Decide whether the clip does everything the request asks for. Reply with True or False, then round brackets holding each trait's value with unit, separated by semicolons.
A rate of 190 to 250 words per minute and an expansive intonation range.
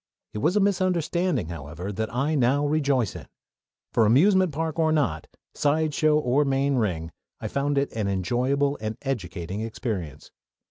False (150 wpm; 6.3 semitones)